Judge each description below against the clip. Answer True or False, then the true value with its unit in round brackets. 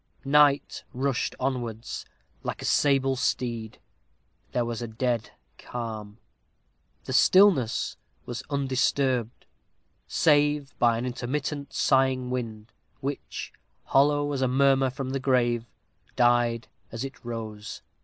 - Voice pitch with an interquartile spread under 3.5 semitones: True (2.7 semitones)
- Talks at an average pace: False (115 wpm)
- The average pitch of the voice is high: False (130 Hz)